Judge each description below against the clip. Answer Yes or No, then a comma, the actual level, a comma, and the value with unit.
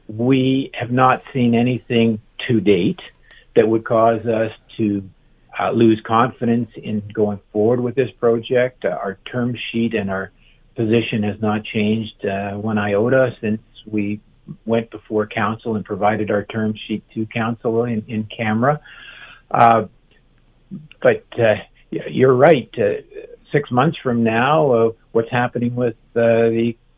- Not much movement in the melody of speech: Yes, narrow, 2.2 semitones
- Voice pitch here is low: Yes, low, 115 Hz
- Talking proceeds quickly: No, average, 145 wpm